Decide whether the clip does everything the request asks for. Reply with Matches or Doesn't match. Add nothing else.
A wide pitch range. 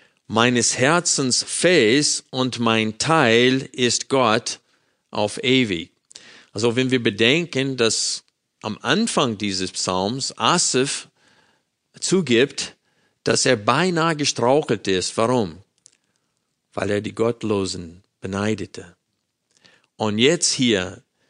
Doesn't match